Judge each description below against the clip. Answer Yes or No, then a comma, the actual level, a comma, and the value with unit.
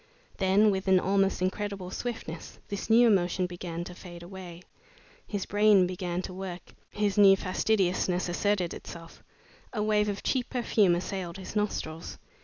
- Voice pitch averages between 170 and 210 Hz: Yes, high, 190 Hz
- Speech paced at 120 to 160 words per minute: Yes, average, 150 wpm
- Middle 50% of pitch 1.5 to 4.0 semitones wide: Yes, narrow, 2.6 semitones